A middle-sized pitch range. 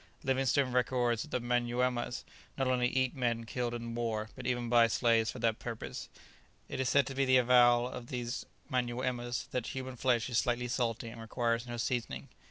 No: narrow, 1.3 semitones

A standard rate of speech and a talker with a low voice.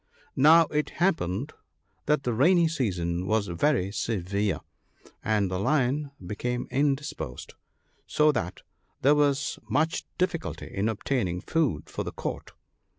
No: slow, 125 wpm; low, 125 Hz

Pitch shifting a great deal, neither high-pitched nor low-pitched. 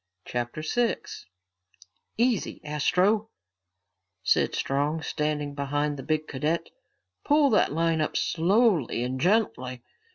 Yes: wide, 6.0 semitones; medium, 155 Hz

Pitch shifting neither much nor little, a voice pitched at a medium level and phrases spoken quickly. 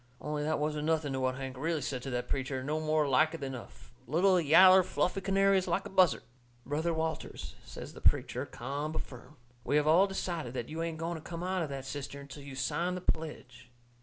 Yes: average, 3.8 semitones; medium, 155 Hz; fast, 225 wpm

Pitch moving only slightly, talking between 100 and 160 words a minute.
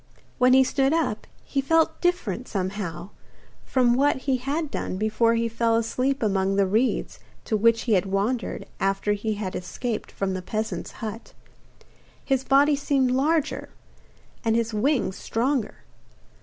No: average, 4.6 semitones; average, 150 wpm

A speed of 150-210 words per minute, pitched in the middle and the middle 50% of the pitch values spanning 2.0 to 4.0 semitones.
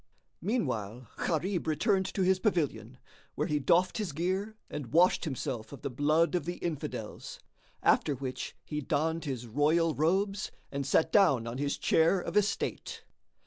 No: average, 155 wpm; medium, 160 Hz; average, 5.0 semitones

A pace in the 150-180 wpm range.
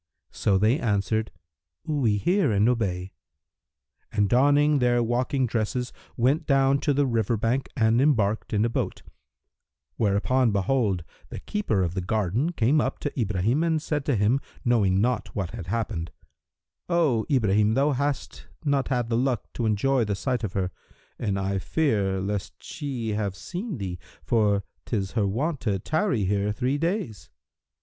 Yes: average, 160 wpm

